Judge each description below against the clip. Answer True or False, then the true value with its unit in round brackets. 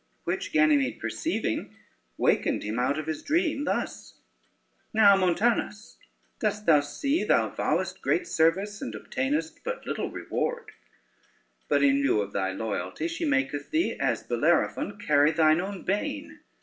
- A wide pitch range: True (8.9 semitones)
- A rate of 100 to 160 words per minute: True (140 wpm)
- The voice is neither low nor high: True (170 Hz)